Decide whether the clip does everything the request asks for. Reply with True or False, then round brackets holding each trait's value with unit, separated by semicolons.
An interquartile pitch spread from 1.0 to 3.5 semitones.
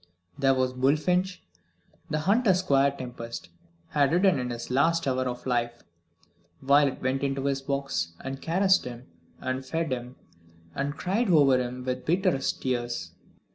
False (3.9 semitones)